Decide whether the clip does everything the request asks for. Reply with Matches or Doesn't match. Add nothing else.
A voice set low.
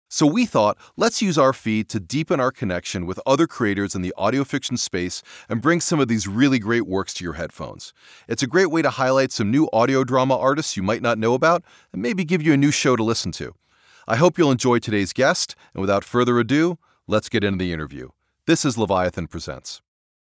Matches